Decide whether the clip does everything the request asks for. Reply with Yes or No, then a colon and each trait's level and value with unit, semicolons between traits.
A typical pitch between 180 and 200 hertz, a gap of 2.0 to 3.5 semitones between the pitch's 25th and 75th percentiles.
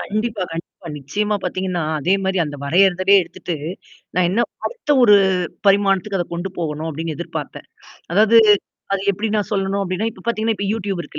Yes: high, 195 Hz; average, 3.1 semitones